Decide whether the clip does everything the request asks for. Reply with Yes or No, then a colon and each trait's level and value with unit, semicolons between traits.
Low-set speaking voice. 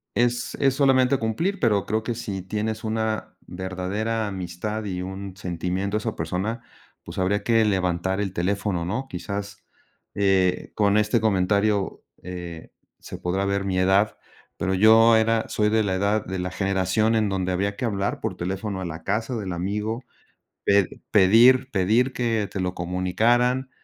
Yes: low, 100 Hz